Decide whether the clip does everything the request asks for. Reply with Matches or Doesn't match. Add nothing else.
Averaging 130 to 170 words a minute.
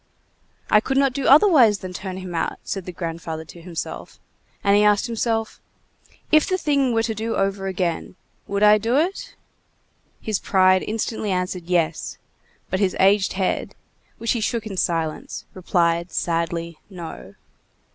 Matches